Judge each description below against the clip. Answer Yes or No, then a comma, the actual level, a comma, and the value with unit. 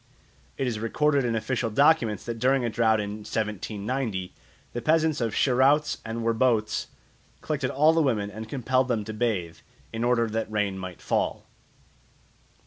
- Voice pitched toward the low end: Yes, low, 115 Hz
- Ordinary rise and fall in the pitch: Yes, average, 3.5 semitones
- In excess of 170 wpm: No, average, 155 wpm